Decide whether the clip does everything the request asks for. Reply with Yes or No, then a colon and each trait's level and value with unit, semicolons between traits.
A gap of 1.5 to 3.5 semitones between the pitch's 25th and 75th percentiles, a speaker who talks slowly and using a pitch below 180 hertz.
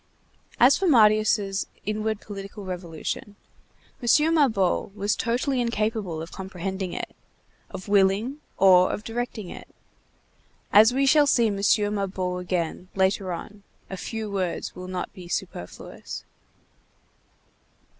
No: average, 3.2 semitones; slow, 120 wpm; high, 200 Hz